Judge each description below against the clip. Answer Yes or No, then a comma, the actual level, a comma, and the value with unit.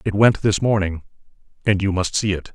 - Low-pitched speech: Yes, low, 100 Hz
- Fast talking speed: Yes, fast, 210 wpm